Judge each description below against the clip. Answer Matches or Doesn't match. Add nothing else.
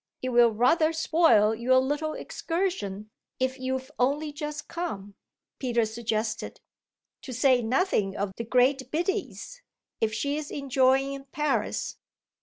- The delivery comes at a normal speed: Doesn't match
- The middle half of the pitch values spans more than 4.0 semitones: Matches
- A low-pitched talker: Doesn't match